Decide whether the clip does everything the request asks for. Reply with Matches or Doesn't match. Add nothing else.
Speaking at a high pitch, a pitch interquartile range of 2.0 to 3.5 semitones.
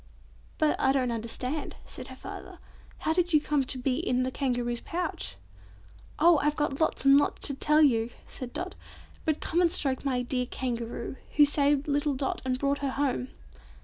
Matches